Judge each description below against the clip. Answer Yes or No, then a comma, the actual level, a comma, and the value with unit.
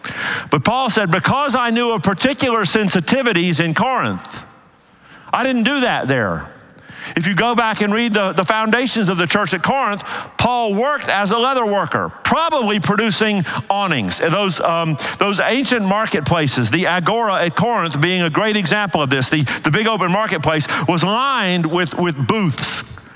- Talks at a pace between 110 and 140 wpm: No, average, 165 wpm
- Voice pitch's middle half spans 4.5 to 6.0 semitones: Yes, average, 5.1 semitones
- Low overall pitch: No, high, 200 Hz